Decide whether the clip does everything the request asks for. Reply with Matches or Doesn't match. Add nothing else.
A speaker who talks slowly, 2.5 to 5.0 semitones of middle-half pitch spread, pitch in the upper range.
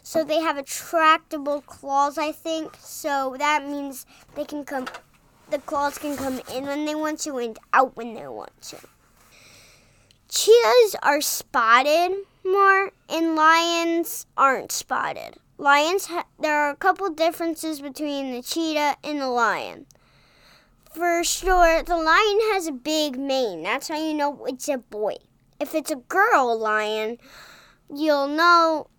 Doesn't match